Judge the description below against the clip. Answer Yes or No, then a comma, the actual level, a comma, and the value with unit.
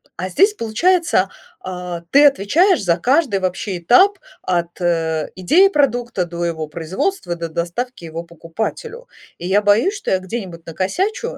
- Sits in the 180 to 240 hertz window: Yes, high, 190 Hz